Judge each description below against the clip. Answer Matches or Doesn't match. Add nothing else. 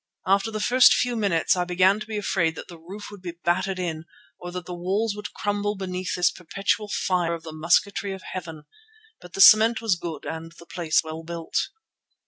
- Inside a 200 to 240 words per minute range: Matches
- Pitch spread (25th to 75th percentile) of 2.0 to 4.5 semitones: Matches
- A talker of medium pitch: Matches